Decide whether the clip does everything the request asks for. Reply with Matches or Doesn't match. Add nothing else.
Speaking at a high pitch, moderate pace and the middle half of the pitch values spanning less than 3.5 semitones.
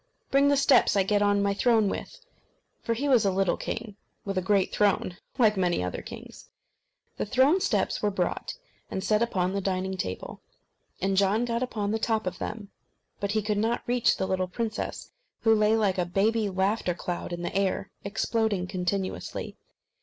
Matches